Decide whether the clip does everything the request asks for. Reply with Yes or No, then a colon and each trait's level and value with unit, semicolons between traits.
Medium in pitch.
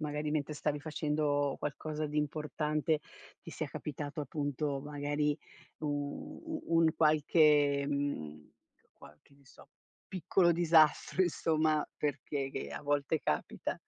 Yes: medium, 150 Hz